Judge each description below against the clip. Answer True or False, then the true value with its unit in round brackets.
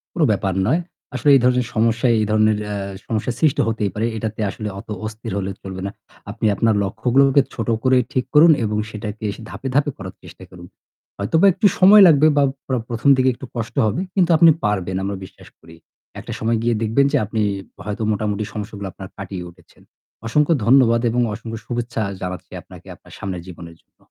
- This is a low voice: True (110 Hz)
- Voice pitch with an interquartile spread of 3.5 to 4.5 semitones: True (4.2 semitones)